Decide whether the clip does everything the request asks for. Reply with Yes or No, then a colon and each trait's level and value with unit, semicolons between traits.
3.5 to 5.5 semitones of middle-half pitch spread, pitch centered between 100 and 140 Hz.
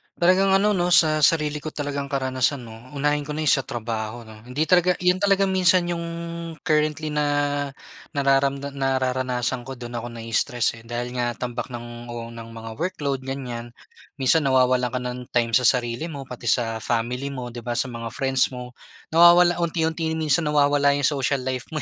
Yes: average, 4.2 semitones; low, 135 Hz